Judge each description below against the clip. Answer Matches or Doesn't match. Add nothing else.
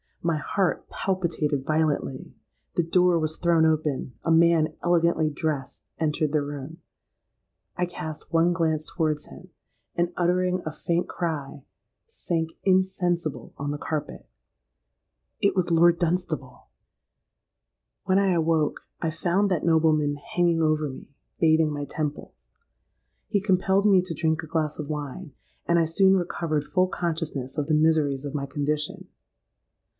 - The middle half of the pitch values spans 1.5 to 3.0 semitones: Matches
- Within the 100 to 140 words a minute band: Matches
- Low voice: Doesn't match